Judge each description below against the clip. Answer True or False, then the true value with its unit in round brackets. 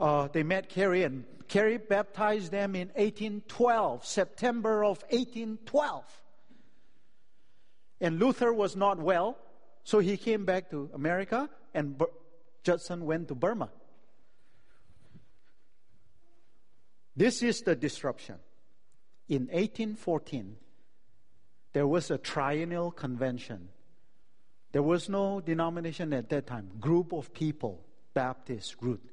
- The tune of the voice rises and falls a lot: True (6.1 semitones)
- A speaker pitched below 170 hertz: False (175 Hz)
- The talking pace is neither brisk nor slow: False (110 wpm)